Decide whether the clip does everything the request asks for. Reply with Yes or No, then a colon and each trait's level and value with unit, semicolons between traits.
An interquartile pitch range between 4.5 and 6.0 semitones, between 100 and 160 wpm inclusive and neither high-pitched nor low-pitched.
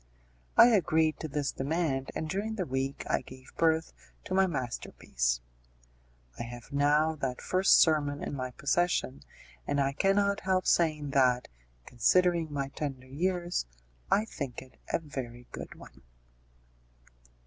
Yes: average, 4.8 semitones; average, 140 wpm; medium, 145 Hz